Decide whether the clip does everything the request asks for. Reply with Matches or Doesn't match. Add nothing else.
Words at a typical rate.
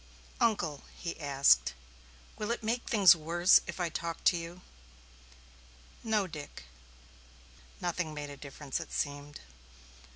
Doesn't match